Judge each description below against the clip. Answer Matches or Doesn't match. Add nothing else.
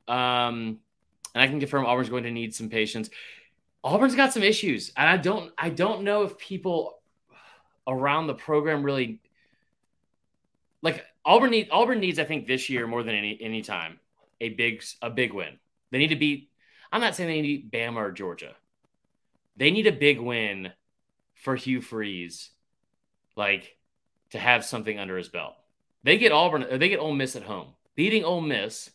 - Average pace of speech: Matches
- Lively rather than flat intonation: Matches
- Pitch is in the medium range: Doesn't match